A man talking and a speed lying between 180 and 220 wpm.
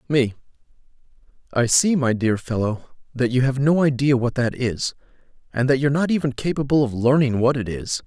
Yes: male; average, 185 wpm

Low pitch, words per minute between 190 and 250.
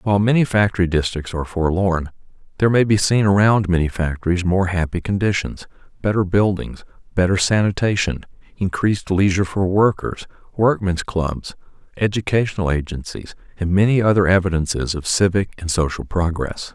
No: very low, 95 Hz; slow, 135 wpm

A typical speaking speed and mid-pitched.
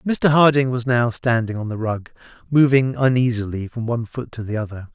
No: average, 195 wpm; low, 120 Hz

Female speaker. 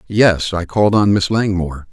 No: male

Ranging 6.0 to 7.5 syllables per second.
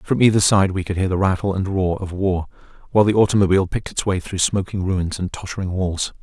Yes: 6.2 syllables/s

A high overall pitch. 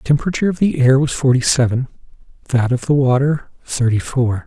No: low, 130 Hz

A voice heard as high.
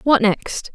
Yes: high, 240 Hz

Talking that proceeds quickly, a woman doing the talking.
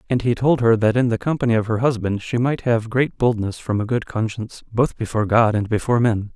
No: fast, 245 wpm; male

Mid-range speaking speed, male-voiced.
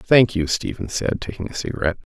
Yes: average, 195 wpm; male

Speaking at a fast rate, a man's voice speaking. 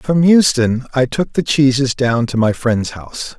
No: average, 195 wpm; male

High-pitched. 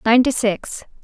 Yes: high, 230 Hz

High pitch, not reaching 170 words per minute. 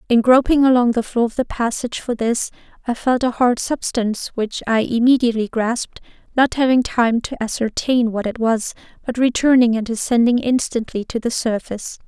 No: high, 235 Hz; average, 175 wpm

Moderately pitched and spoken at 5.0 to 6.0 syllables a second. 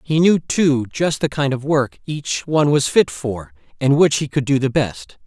No: medium, 145 Hz; 4.4 syllables/s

